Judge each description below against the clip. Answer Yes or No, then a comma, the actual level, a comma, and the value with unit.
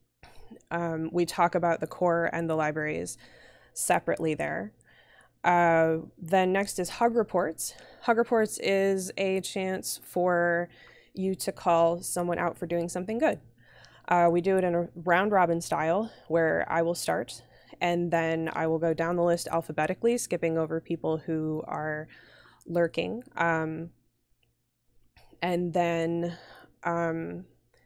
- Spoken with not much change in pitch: Yes, narrow, 1.9 semitones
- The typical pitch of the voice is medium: Yes, medium, 170 Hz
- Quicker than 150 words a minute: No, average, 140 wpm